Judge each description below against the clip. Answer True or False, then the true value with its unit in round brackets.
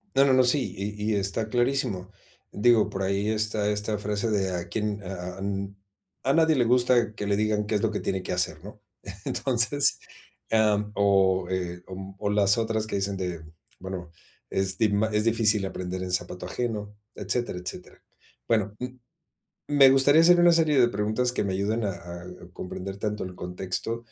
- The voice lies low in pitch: True (105 Hz)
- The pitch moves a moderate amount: True (3.2 semitones)